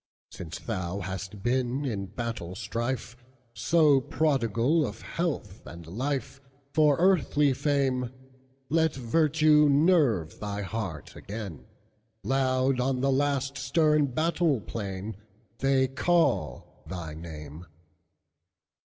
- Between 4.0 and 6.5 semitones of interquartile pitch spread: Yes, wide, 5.4 semitones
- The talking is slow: Yes, slow, 90 wpm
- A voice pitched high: No, low, 130 Hz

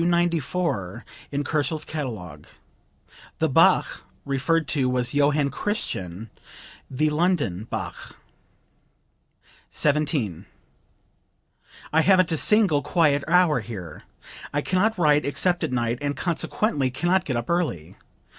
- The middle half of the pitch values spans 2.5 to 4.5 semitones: No, average, 5.3 semitones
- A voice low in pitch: No, medium, 145 Hz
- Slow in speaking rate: Yes, slow, 115 wpm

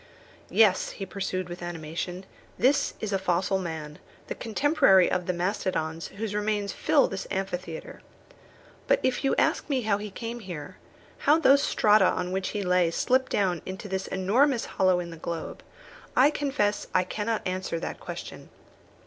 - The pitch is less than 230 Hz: Yes, high, 190 Hz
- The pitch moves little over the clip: No, average, 3.6 semitones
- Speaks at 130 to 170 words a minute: Yes, average, 165 wpm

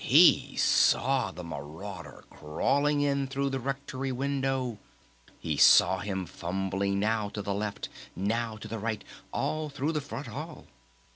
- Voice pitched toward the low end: Yes, low, 115 Hz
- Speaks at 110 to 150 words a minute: Yes, average, 145 wpm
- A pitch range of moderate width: No, wide, 5.8 semitones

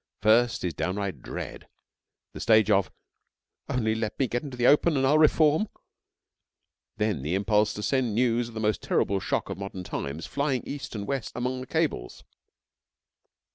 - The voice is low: Yes, low, 110 Hz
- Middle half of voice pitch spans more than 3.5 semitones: Yes, average, 4.5 semitones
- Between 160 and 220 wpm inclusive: Yes, average, 170 wpm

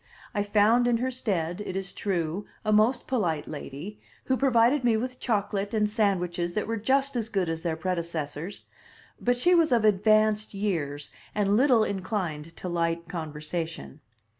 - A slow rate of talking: No, average, 165 wpm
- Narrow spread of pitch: No, average, 5.2 semitones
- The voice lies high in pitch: Yes, high, 205 Hz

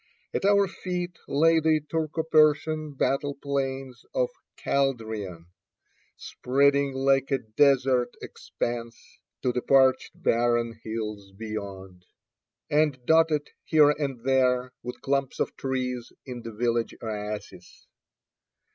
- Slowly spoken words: Yes, slow, 110 wpm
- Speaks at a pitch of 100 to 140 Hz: Yes, low, 135 Hz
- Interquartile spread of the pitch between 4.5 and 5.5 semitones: No, average, 4.0 semitones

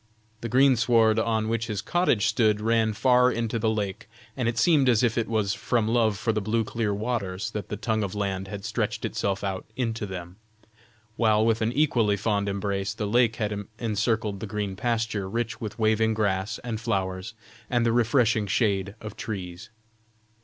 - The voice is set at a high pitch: No, low, 110 Hz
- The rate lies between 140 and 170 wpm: No, average, 180 wpm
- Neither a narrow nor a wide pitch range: No, narrow, 2.3 semitones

